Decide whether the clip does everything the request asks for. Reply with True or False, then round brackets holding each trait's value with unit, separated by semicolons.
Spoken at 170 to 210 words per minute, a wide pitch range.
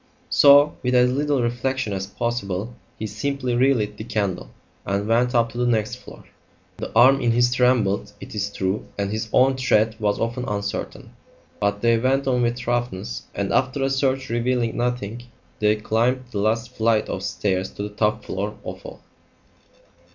False (175 wpm; 3.1 semitones)